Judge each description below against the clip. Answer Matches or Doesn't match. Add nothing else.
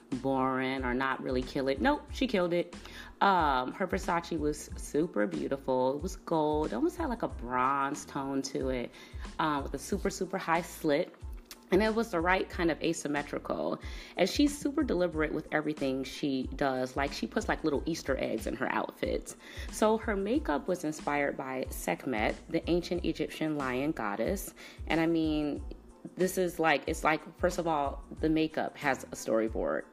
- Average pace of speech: Matches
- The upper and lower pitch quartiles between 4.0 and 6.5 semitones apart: Matches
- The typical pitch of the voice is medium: Matches